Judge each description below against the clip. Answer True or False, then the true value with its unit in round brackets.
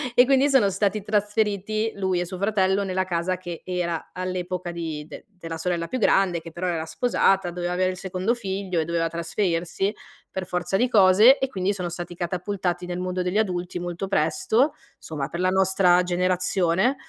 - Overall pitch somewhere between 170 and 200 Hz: True (185 Hz)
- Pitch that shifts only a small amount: True (2.3 semitones)